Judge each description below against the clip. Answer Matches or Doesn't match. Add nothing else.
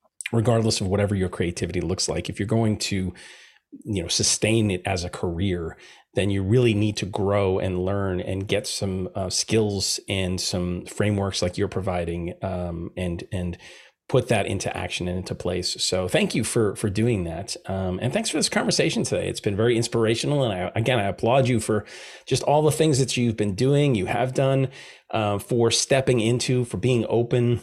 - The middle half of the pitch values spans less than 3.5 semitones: Doesn't match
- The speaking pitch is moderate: Doesn't match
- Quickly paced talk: Doesn't match